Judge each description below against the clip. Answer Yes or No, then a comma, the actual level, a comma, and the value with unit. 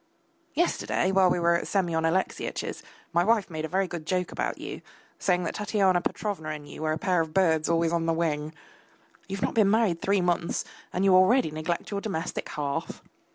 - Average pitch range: Yes, average, 3.0 semitones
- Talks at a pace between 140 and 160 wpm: No, average, 200 wpm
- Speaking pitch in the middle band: Yes, medium, 175 Hz